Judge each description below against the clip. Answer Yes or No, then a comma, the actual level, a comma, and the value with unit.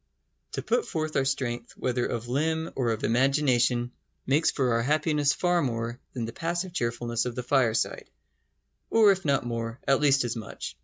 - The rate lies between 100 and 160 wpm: No, average, 175 wpm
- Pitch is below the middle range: Yes, low, 130 Hz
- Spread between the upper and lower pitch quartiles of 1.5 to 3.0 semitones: No, average, 4.2 semitones